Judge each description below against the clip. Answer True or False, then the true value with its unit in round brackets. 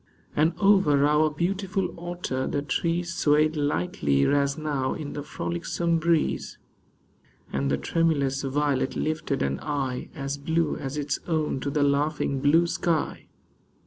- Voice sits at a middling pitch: True (150 Hz)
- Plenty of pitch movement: False (3.0 semitones)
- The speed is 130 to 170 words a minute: True (140 wpm)